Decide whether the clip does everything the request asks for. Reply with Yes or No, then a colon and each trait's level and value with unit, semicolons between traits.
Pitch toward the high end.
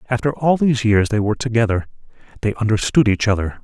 No: low, 115 Hz